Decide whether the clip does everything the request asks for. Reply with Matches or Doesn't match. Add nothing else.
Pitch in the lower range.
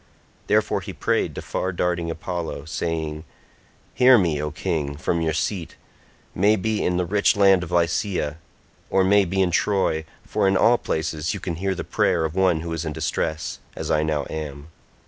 Matches